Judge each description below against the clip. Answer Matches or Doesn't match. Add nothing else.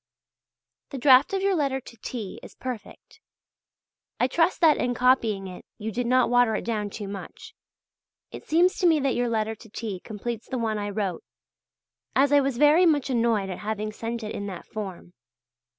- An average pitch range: Matches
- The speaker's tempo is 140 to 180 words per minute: Doesn't match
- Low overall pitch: Doesn't match